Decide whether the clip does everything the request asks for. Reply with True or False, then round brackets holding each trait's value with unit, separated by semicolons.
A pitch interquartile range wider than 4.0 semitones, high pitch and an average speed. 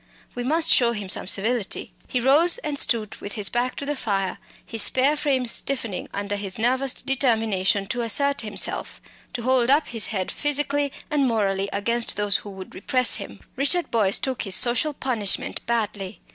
True (4.8 semitones; 235 Hz; 175 wpm)